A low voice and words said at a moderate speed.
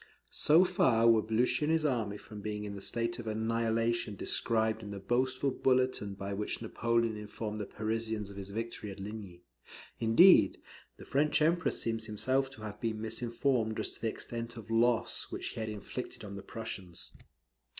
Yes: low, 115 Hz; average, 180 wpm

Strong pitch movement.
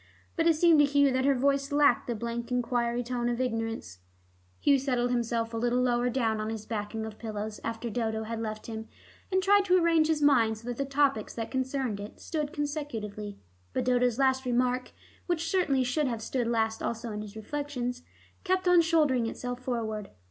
No: average, 4.0 semitones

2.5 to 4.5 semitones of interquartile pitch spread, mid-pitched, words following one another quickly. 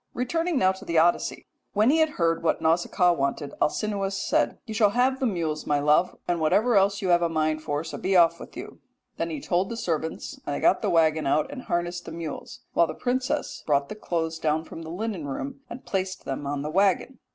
No: average, 5.1 semitones; medium, 175 Hz; fast, 230 wpm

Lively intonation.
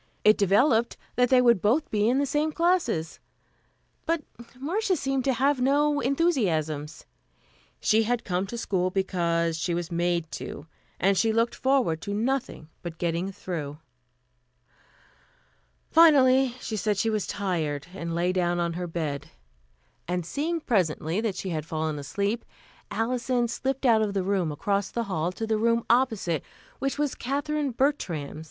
Yes: wide, 7.3 semitones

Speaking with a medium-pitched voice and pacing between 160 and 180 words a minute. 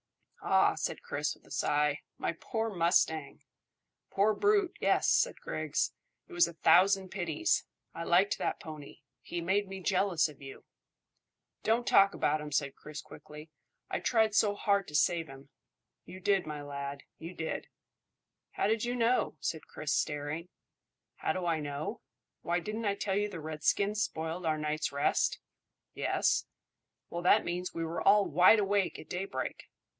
Yes: medium, 175 Hz; average, 165 wpm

